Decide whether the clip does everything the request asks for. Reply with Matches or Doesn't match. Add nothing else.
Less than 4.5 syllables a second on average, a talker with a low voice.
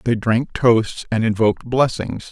Matches